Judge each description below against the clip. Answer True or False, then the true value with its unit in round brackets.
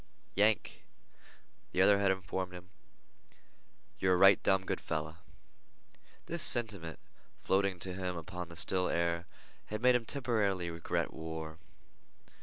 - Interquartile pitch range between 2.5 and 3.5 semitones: True (2.8 semitones)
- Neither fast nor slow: False (130 wpm)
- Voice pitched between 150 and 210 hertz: False (95 Hz)